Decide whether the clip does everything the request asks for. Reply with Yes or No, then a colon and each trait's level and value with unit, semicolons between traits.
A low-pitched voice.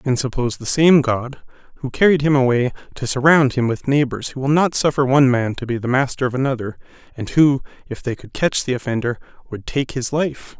Yes: low, 130 Hz